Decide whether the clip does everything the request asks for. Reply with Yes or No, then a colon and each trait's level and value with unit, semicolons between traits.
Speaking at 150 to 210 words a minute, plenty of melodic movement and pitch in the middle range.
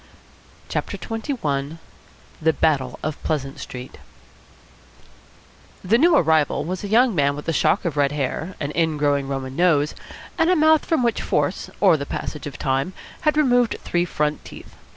Yes: average, 160 wpm; wide, 7.8 semitones; medium, 160 Hz